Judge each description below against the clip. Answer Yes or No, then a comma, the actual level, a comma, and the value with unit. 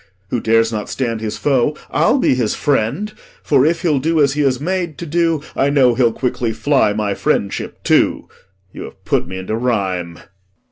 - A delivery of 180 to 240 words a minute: Yes, average, 190 wpm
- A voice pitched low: Yes, low, 130 Hz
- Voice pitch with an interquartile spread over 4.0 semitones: Yes, average, 5.2 semitones